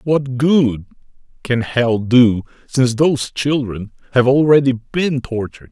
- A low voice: Yes, low, 125 Hz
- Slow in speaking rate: Yes, slow, 125 wpm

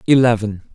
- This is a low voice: Yes, low, 115 Hz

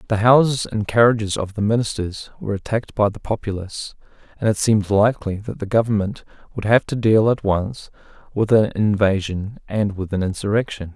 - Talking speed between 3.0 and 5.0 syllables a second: No, 5.6 syllables/s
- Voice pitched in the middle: No, low, 105 Hz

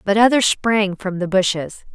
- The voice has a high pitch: Yes, high, 200 Hz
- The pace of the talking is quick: No, average, 185 wpm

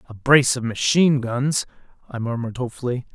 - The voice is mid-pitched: No, low, 125 Hz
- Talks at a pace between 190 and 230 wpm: No, average, 150 wpm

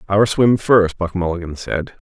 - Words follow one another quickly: No, average, 175 wpm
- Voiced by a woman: No, male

